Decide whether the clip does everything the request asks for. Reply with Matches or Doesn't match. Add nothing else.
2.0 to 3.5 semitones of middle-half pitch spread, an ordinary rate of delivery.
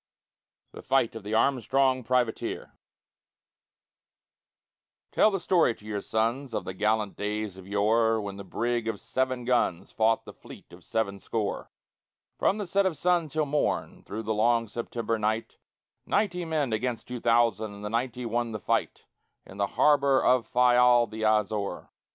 Matches